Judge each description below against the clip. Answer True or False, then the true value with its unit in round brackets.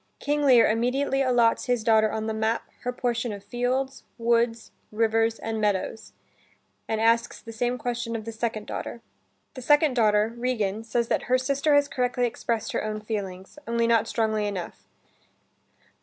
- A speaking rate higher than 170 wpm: False (165 wpm)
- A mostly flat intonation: True (2.3 semitones)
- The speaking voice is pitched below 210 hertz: False (230 Hz)